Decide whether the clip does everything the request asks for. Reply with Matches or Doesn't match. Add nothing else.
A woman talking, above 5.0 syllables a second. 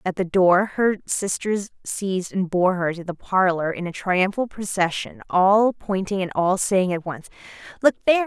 Doesn't match